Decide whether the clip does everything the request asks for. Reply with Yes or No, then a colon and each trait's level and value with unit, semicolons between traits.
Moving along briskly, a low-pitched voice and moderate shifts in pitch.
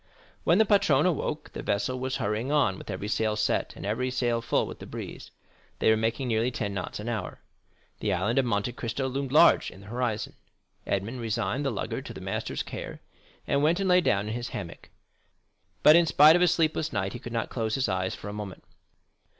Yes: fast, 215 wpm; low, 120 Hz; average, 5.0 semitones